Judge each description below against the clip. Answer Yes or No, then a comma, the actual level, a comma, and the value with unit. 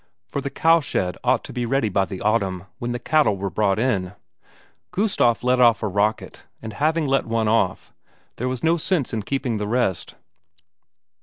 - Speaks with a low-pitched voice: Yes, low, 120 Hz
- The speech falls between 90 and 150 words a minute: No, average, 180 wpm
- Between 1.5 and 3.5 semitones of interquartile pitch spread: No, average, 4.8 semitones